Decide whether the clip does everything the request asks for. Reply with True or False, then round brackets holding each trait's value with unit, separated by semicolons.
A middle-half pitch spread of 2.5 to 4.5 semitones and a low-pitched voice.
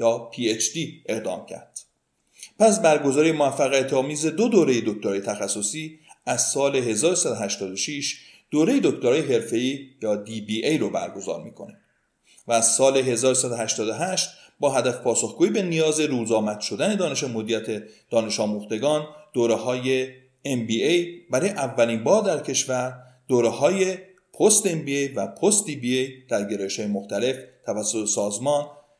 False (5.1 semitones; 130 Hz)